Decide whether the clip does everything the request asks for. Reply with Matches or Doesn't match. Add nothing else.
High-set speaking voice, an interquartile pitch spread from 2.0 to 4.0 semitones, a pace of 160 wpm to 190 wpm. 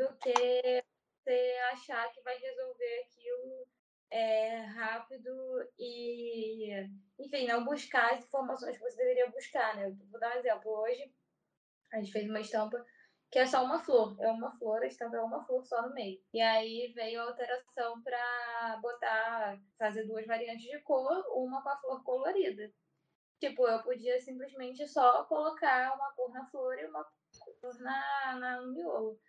Matches